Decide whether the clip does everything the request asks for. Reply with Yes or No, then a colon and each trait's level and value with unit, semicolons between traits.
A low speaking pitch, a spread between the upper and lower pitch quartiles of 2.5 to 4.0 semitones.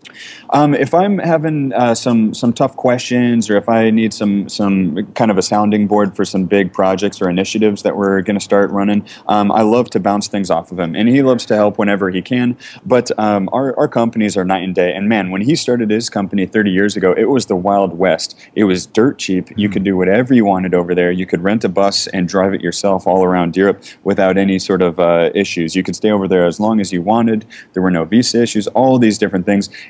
Yes: low, 100 Hz; average, 3.0 semitones